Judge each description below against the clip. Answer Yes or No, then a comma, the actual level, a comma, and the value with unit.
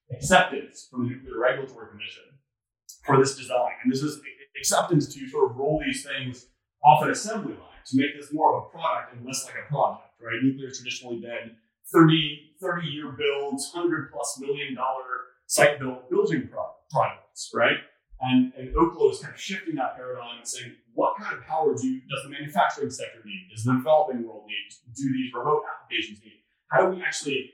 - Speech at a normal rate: Yes, average, 190 wpm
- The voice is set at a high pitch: No, low, 135 Hz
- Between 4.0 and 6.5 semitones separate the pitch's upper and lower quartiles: No, average, 3.5 semitones